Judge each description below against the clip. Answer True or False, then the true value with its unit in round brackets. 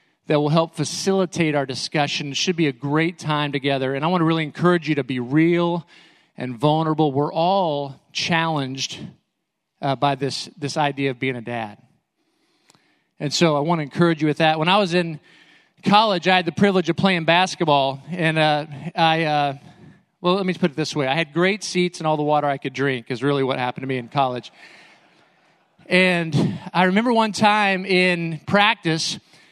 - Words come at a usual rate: True (190 wpm)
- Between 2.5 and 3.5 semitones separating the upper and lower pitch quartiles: False (3.9 semitones)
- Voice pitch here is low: False (160 Hz)